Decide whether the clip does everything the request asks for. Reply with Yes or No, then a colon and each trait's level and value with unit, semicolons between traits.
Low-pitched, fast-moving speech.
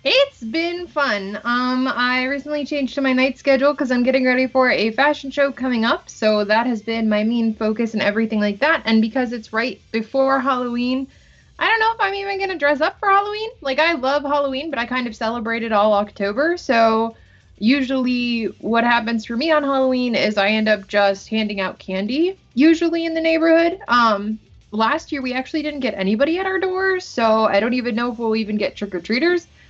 No: very high, 255 Hz; fast, 210 wpm